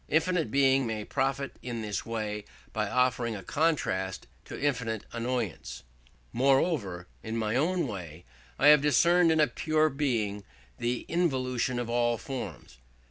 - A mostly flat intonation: No, average, 5.1 semitones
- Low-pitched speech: Yes, low, 125 Hz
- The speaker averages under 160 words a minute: Yes, slow, 135 wpm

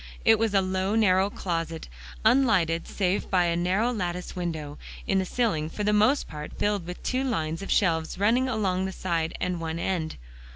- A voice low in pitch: No, medium, 185 Hz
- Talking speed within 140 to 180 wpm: No, average, 190 wpm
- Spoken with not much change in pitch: No, average, 3.9 semitones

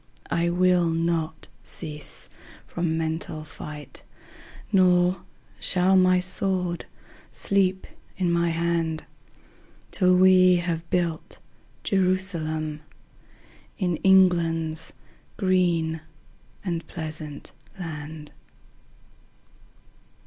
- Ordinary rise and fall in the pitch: No, narrow, 2.3 semitones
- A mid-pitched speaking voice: Yes, medium, 170 Hz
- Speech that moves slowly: Yes, slow, 75 wpm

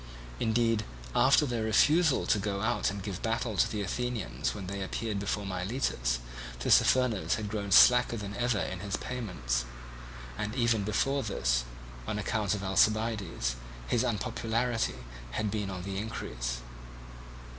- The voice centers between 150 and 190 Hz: No, low, 105 Hz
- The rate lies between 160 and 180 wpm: No, average, 145 wpm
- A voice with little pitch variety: No, average, 3.2 semitones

